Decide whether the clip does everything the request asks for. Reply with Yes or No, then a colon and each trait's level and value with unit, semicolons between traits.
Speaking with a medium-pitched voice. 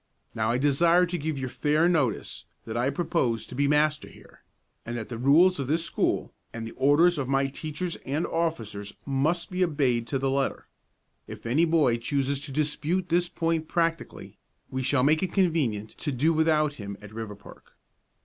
Yes: medium, 145 Hz